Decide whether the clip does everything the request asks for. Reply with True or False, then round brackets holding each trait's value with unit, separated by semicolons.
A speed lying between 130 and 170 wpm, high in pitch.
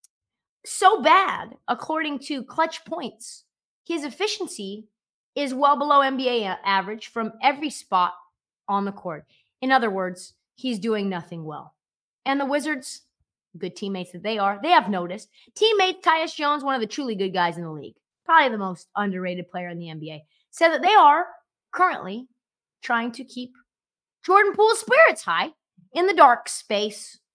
True (160 wpm; 240 Hz)